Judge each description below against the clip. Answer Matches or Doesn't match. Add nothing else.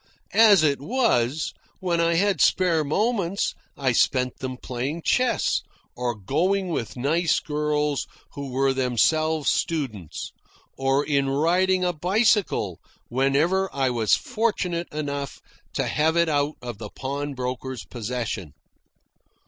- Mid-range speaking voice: Matches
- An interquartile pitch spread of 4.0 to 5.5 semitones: Matches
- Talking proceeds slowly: Matches